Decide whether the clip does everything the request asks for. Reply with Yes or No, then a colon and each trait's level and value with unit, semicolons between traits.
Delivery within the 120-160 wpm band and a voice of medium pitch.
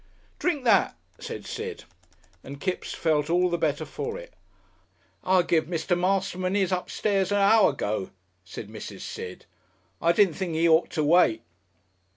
Yes: average, 155 wpm; medium, 180 Hz